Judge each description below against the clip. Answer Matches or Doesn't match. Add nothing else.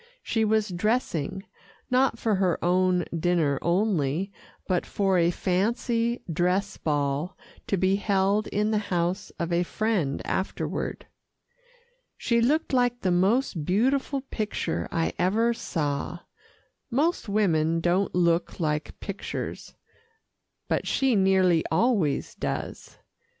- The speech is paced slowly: Matches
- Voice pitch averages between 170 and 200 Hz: Matches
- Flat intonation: Doesn't match